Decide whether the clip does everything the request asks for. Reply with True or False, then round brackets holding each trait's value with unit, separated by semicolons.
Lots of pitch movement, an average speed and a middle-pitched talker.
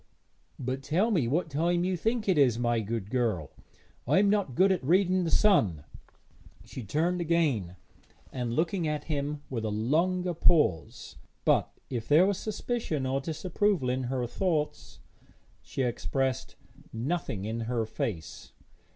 True (7.0 semitones; 150 wpm; 145 Hz)